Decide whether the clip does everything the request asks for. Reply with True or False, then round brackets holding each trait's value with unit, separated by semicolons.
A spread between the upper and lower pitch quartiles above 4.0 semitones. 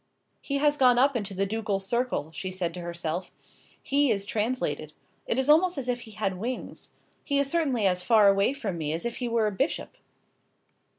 True (5.4 semitones)